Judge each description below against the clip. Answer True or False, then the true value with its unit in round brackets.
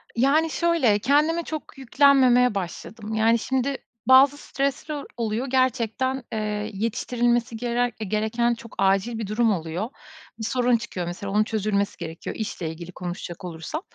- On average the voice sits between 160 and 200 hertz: False (230 Hz)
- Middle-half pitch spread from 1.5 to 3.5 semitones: False (4.0 semitones)